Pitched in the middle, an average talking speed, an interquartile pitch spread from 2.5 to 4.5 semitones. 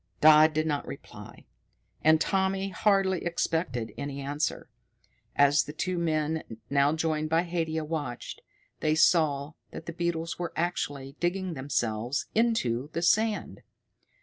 No: medium, 160 Hz; slow, 130 wpm; average, 3.3 semitones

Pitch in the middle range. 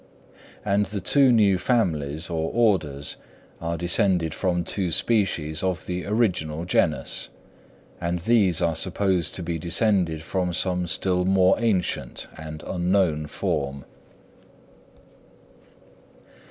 No: very low, 90 Hz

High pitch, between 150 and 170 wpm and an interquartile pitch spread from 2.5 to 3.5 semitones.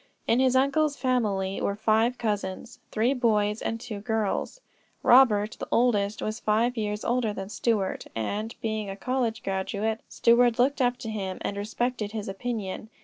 Yes: high, 220 Hz; average, 160 wpm; average, 3.0 semitones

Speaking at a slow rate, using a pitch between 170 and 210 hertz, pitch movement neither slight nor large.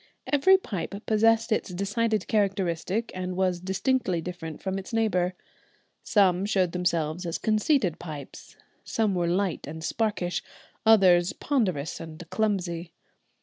Yes: slow, 125 wpm; medium, 185 Hz; average, 3.7 semitones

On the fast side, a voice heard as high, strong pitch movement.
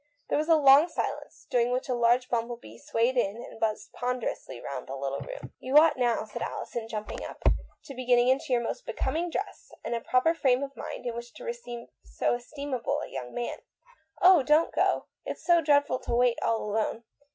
No: fast, 220 wpm; high, 245 Hz; average, 3.9 semitones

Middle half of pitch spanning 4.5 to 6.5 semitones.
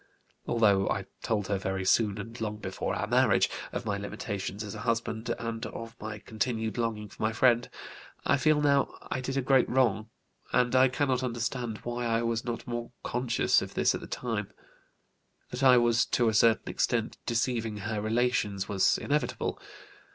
No: narrow, 2.6 semitones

